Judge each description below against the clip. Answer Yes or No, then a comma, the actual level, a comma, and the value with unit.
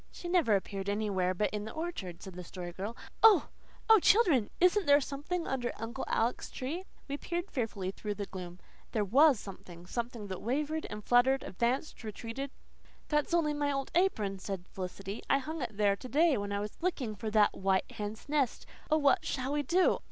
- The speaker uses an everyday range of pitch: No, wide, 6.7 semitones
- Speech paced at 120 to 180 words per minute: No, average, 195 wpm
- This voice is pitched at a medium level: No, high, 240 Hz